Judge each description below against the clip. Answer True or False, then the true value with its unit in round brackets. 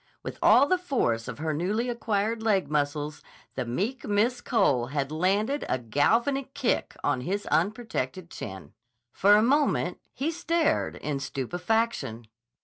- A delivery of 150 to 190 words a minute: False (140 wpm)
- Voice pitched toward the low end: False (200 Hz)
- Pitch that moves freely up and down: True (8.7 semitones)